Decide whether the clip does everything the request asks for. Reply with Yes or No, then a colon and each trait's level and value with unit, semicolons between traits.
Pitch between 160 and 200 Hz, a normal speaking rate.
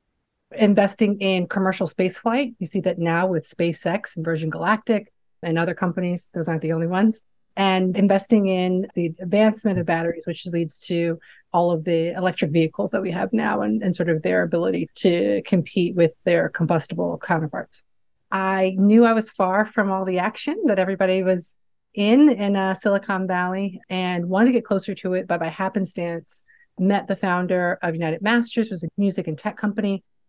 Yes: medium, 185 Hz; average, 180 wpm